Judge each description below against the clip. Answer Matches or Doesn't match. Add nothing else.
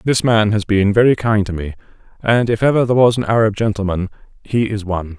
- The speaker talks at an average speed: Doesn't match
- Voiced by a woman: Doesn't match